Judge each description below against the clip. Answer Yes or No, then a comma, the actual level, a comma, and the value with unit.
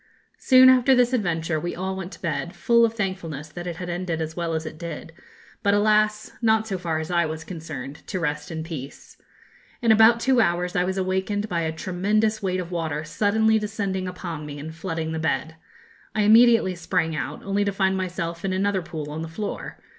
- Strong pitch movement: No, average, 4.3 semitones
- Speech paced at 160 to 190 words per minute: No, fast, 205 wpm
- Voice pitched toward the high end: No, medium, 180 Hz